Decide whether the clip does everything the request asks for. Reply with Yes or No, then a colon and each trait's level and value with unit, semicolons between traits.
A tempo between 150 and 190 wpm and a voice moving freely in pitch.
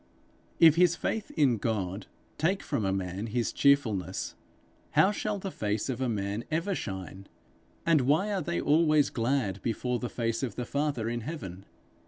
Yes: average, 170 wpm; wide, 7.2 semitones